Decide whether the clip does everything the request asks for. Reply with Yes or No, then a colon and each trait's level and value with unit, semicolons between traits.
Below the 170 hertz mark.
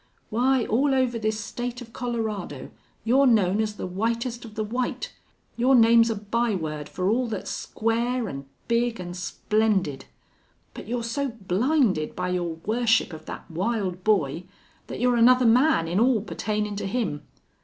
No: high, 225 Hz